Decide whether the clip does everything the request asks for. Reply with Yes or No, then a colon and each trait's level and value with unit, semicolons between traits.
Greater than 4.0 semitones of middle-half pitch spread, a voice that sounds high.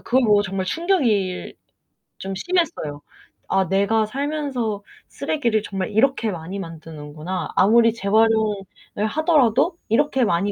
Yes: wide, 5.5 semitones; high, 215 Hz